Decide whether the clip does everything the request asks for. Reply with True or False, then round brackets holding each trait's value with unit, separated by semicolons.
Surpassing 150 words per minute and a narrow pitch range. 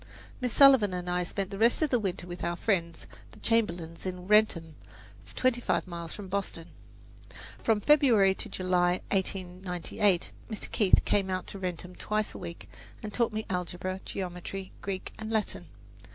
False (165 wpm; 3.2 semitones)